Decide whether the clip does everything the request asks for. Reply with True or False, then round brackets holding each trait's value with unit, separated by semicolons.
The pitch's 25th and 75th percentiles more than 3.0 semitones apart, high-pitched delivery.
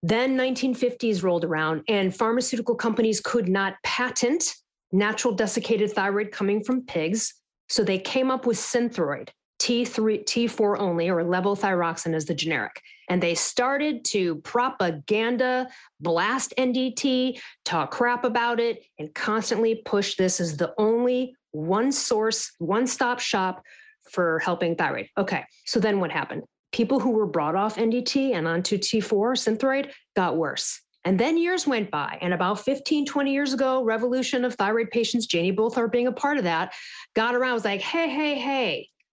True (4.6 semitones; 230 Hz)